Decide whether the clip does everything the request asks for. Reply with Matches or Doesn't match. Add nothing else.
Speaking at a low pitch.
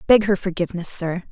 Doesn't match